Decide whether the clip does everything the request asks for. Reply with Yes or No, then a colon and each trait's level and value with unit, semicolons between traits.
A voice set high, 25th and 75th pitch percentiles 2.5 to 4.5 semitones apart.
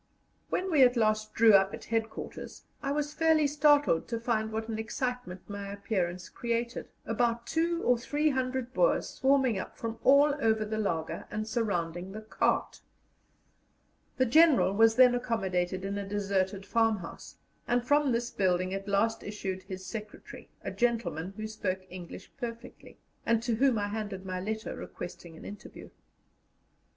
Yes: high, 220 Hz; average, 4.0 semitones